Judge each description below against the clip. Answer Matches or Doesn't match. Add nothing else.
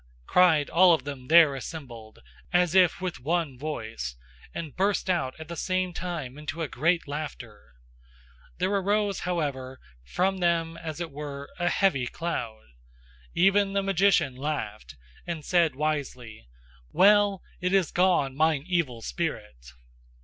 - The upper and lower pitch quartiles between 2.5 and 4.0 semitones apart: Doesn't match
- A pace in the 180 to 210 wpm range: Doesn't match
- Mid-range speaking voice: Matches